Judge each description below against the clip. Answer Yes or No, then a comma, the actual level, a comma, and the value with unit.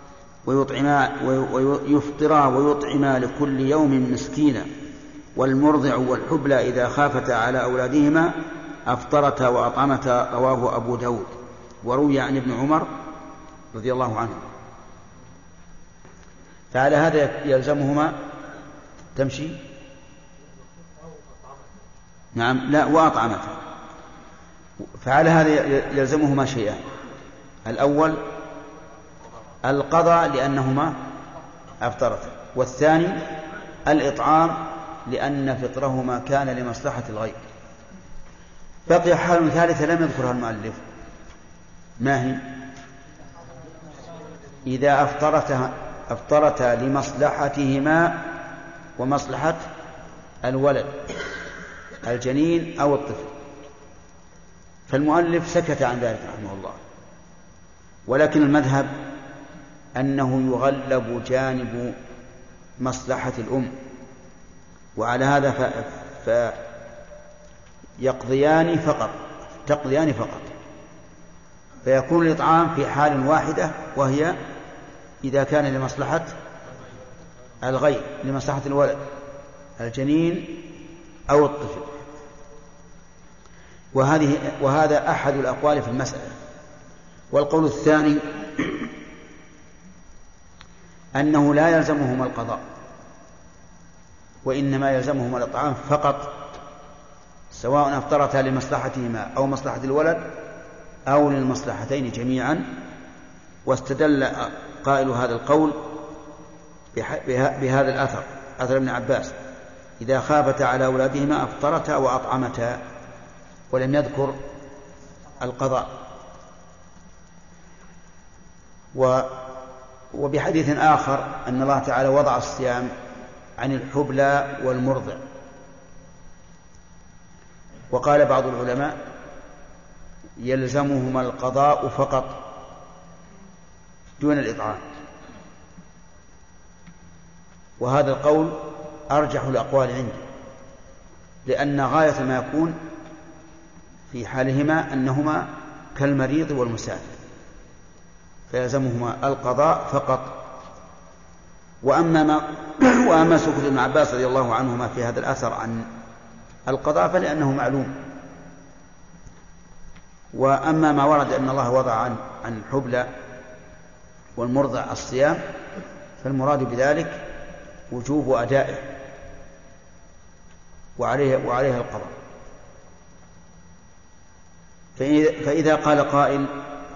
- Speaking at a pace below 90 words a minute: Yes, average, 75 wpm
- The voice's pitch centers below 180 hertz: Yes, medium, 140 Hz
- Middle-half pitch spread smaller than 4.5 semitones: Yes, average, 2.7 semitones